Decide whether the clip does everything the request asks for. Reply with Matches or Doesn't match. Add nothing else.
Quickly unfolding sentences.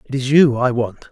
Matches